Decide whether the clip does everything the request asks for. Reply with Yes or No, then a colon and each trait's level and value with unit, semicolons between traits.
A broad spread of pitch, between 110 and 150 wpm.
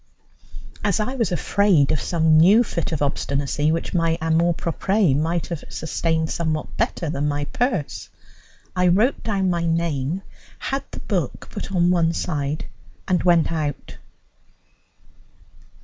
No: average, 2.9 semitones; average, 140 wpm